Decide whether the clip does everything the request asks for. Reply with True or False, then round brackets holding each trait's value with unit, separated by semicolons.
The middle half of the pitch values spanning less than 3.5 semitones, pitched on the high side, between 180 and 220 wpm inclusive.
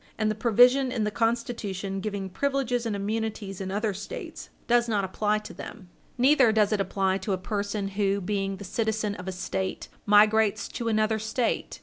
True (2.6 semitones; 210 Hz; 185 wpm)